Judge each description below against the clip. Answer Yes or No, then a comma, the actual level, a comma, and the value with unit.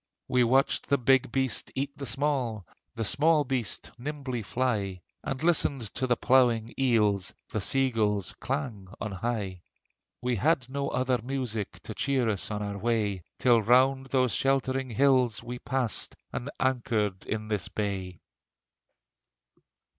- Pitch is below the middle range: Yes, low, 125 Hz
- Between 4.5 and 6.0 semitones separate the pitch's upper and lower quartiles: No, average, 3.8 semitones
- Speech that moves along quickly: No, average, 145 wpm